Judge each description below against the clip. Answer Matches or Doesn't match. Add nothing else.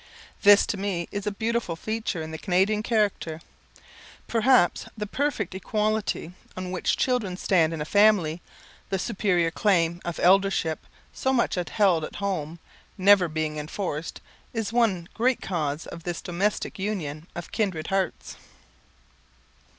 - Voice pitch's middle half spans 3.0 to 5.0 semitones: Matches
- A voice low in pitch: Doesn't match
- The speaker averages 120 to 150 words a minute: Matches